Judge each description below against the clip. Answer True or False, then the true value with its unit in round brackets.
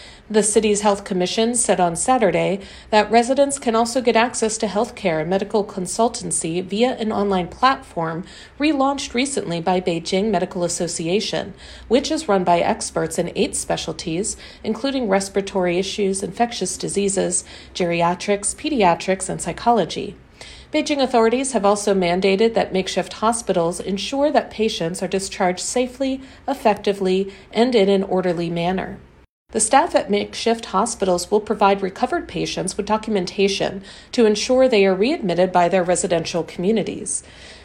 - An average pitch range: True (3.8 semitones)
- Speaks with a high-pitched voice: True (200 Hz)